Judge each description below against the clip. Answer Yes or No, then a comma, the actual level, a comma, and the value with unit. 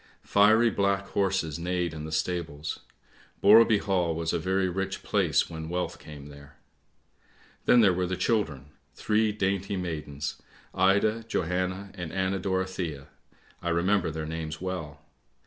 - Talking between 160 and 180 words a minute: No, average, 145 wpm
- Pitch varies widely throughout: No, average, 3.6 semitones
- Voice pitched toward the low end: Yes, very low, 90 Hz